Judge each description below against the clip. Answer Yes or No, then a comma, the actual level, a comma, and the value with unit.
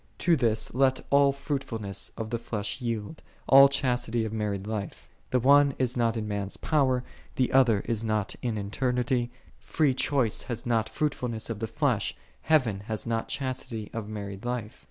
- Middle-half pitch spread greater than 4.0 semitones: No, average, 3.3 semitones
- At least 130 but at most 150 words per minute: No, average, 170 wpm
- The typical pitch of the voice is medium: No, low, 115 Hz